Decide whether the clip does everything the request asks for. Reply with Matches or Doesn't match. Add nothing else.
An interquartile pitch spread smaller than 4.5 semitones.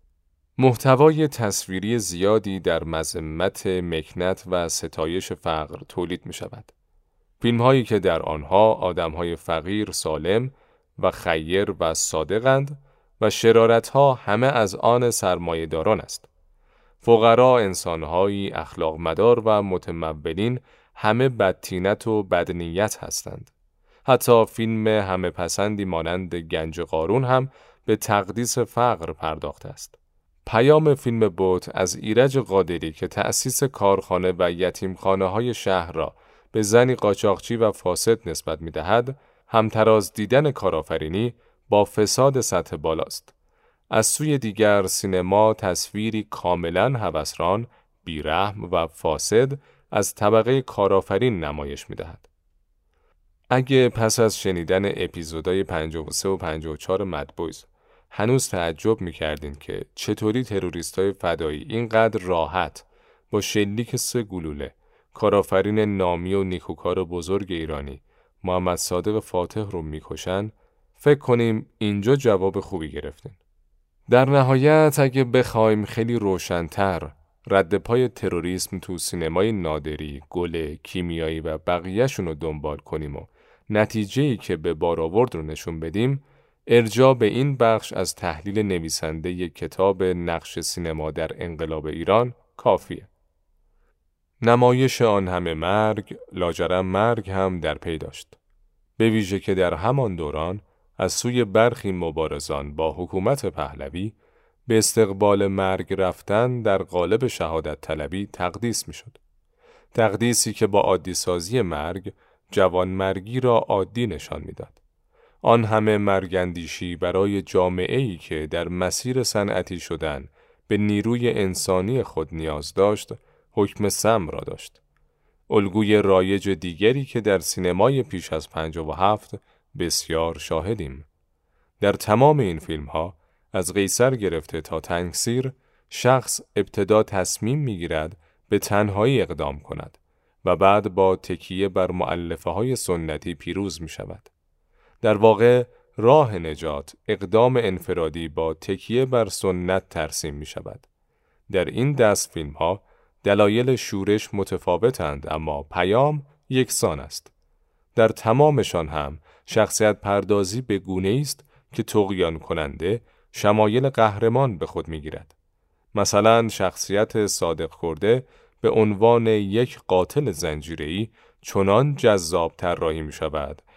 Doesn't match